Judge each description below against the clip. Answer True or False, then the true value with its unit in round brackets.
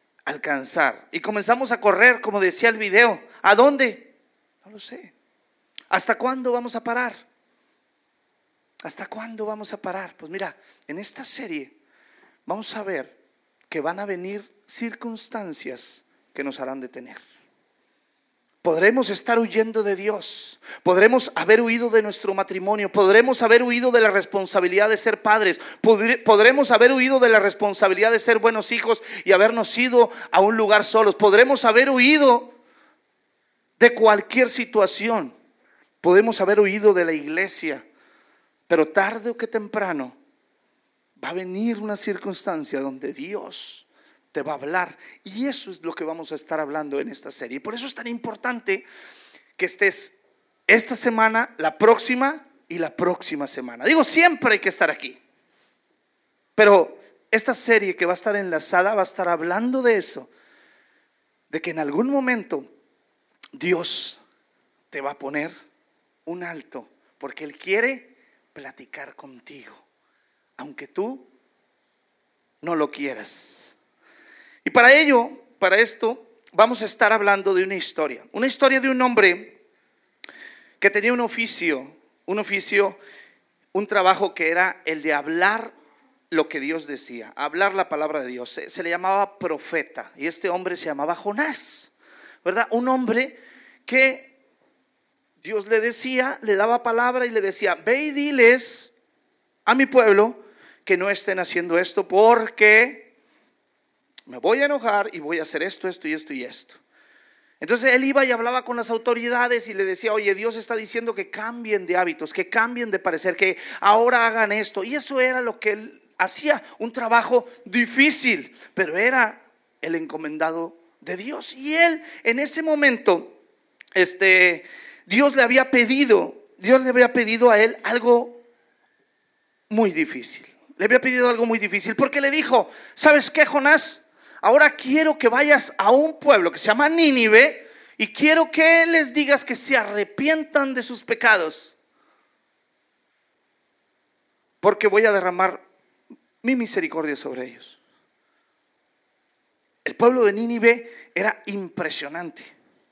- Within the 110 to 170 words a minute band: True (145 wpm)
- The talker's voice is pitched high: True (225 Hz)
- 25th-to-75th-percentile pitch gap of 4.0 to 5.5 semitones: True (4.6 semitones)